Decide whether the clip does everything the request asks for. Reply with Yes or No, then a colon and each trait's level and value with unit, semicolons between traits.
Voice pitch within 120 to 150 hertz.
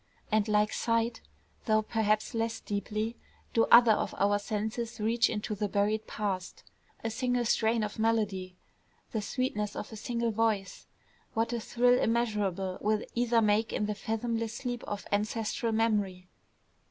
No: high, 220 Hz